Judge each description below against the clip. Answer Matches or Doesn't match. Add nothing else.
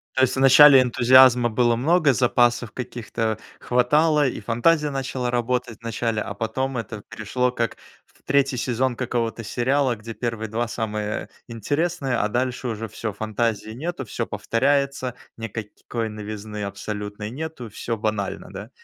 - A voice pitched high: Doesn't match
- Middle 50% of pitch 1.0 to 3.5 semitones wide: Matches